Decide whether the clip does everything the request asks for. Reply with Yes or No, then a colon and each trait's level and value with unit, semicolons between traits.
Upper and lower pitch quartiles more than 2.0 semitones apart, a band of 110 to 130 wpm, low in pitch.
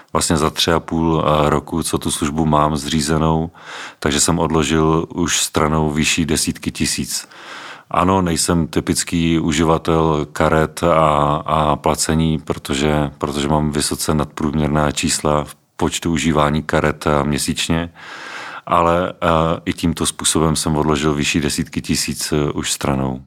No: narrow, 1.6 semitones; average, 125 wpm; very low, 80 Hz